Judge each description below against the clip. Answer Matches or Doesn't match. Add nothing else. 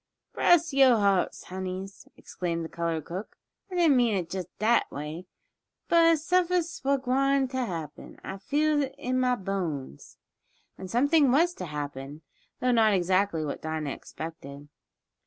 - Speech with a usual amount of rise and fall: Doesn't match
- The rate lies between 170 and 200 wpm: Doesn't match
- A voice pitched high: Matches